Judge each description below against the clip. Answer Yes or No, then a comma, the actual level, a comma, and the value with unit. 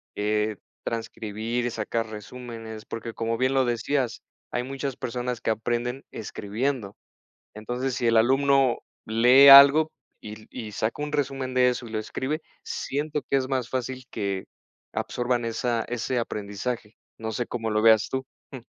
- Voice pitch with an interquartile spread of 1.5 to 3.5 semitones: Yes, average, 2.8 semitones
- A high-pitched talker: No, low, 120 Hz